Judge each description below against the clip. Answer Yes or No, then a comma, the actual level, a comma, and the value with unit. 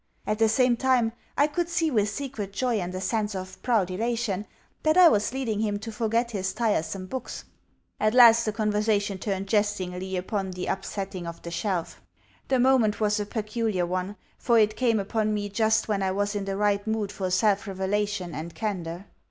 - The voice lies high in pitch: Yes, high, 210 Hz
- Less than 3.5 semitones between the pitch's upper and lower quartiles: Yes, average, 2.9 semitones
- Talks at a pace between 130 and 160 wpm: No, average, 195 wpm